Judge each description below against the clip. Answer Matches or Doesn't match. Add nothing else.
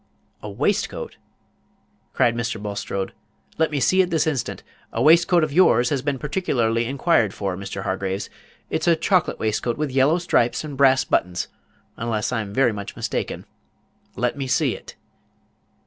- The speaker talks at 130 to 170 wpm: Matches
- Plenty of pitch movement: Matches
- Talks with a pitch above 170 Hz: Doesn't match